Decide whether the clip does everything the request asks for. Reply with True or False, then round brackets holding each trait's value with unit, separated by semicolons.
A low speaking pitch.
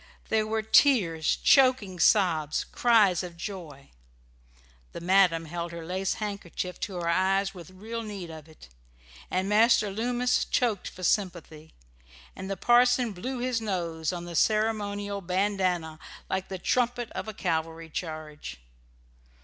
False (190 Hz)